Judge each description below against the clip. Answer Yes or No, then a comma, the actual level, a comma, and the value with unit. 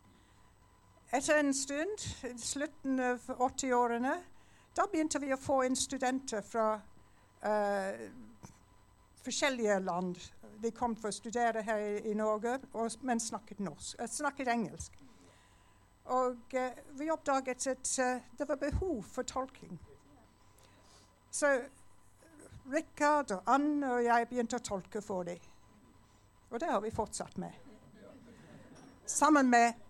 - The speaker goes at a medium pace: No, slow, 125 wpm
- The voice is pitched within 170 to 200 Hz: No, high, 240 Hz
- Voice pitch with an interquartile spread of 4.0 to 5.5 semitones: Yes, average, 5.0 semitones